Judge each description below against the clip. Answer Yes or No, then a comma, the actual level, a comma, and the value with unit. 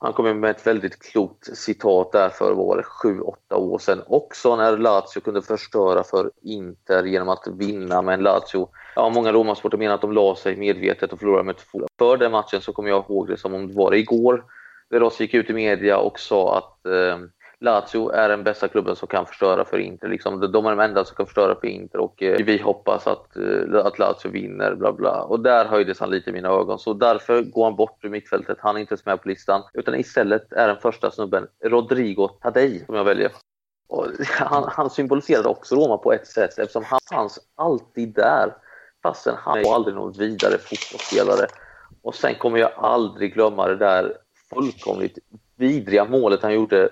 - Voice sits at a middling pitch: No, low, 110 Hz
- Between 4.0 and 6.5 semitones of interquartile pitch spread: Yes, average, 4.8 semitones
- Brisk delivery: Yes, fast, 200 wpm